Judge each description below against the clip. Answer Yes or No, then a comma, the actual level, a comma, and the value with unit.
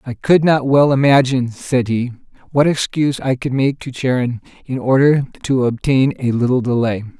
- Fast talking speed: No, average, 175 wpm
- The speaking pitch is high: No, low, 130 Hz